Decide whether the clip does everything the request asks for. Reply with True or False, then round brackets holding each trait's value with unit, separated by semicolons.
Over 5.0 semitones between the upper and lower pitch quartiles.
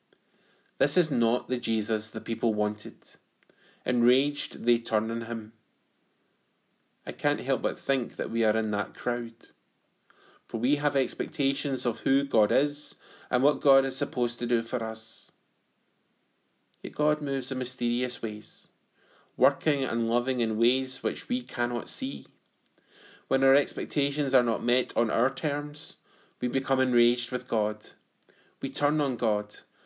False (3.0 semitones)